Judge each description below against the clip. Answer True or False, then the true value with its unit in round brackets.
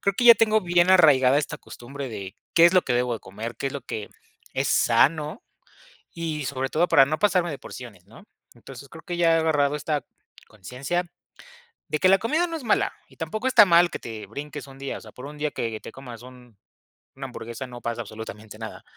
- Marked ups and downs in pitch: True (6.1 semitones)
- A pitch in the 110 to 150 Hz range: True (140 Hz)